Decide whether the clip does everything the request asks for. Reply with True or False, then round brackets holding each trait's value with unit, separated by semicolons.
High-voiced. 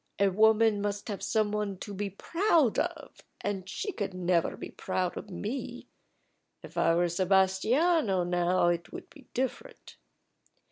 True (200 Hz)